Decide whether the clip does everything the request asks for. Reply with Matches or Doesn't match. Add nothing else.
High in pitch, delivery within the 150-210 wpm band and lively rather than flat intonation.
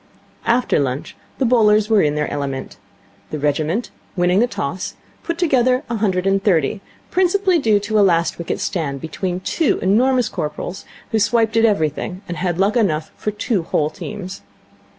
Matches